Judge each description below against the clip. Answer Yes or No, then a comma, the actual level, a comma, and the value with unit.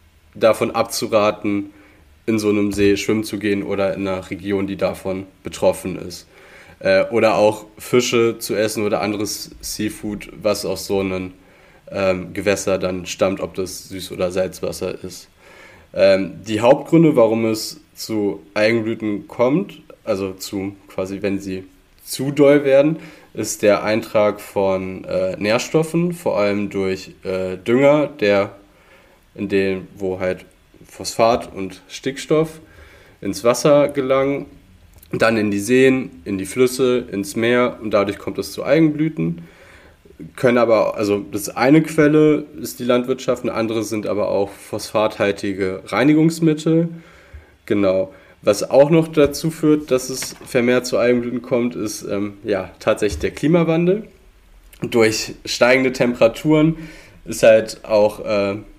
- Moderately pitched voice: No, low, 105 Hz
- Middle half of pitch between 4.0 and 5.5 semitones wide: Yes, average, 5.2 semitones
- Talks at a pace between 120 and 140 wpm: Yes, average, 130 wpm